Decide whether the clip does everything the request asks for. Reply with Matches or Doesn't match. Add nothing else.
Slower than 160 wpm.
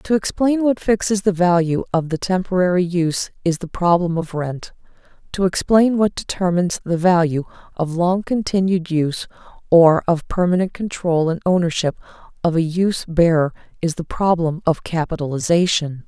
Matches